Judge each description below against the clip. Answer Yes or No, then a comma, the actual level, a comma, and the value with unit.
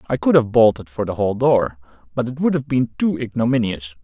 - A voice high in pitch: No, low, 120 Hz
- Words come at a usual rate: No, fast, 225 wpm